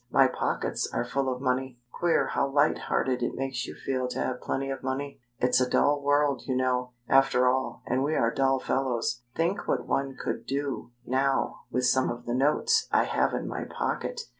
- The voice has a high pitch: No, low, 130 Hz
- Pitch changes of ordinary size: No, narrow, 1.6 semitones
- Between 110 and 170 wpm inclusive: No, average, 200 wpm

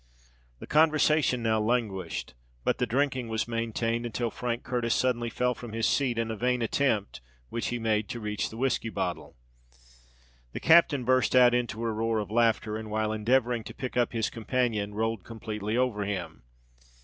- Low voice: Yes, low, 115 Hz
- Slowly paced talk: No, average, 175 wpm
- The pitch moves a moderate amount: No, narrow, 2.3 semitones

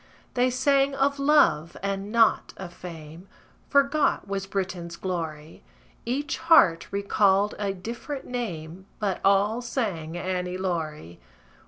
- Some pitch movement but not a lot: No, wide, 6.2 semitones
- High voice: Yes, high, 195 Hz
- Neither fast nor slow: No, slow, 120 wpm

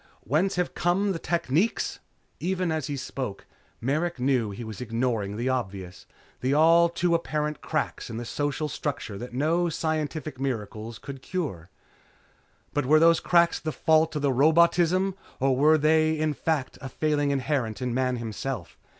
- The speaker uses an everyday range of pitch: Yes, average, 4.4 semitones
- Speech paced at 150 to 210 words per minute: Yes, average, 160 wpm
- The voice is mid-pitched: Yes, medium, 145 Hz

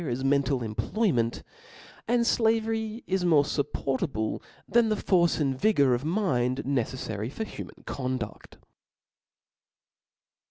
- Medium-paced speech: No, slow, 110 wpm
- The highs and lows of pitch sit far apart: Yes, wide, 9.0 semitones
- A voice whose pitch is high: No, medium, 140 Hz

